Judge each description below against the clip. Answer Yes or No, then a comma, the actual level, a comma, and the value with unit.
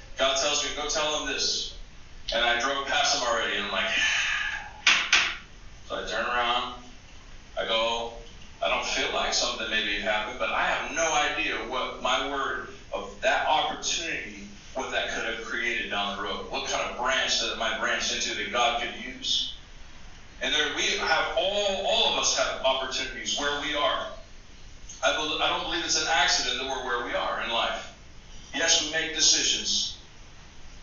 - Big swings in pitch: Yes, wide, 7.1 semitones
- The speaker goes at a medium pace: No, fast, 180 wpm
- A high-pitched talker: No, low, 120 Hz